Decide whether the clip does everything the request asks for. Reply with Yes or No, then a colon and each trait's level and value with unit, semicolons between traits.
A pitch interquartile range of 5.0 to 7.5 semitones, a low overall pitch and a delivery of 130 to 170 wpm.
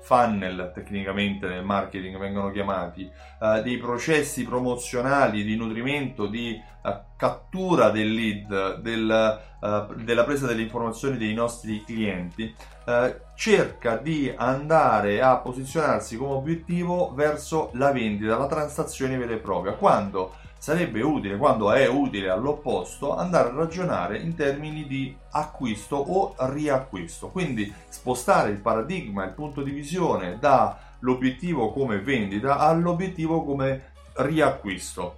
No: wide, 5.5 semitones; low, 120 Hz; average, 120 wpm